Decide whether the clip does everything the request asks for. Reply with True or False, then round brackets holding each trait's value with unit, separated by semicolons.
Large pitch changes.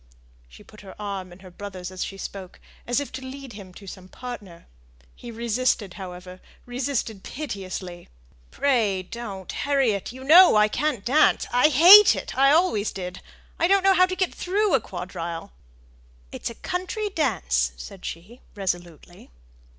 True (7.1 semitones)